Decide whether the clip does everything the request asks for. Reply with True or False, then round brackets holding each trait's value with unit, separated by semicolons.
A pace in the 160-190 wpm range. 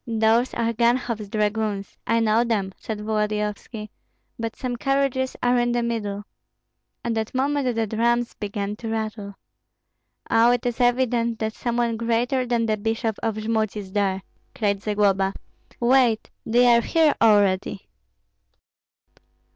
False (140 wpm)